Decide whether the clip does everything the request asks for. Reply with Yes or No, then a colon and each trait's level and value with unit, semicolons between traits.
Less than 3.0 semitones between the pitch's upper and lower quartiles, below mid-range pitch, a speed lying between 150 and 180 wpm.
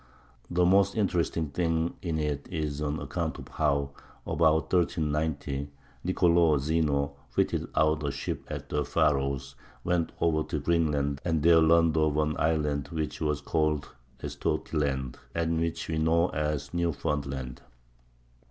No: narrow, 2.5 semitones; very low, 75 Hz; slow, 135 wpm